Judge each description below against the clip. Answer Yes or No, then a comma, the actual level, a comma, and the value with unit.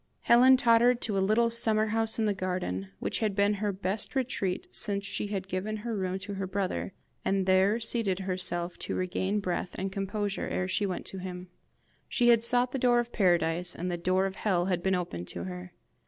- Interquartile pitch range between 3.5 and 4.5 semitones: No, average, 3.1 semitones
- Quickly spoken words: Yes, fast, 210 wpm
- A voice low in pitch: No, high, 195 Hz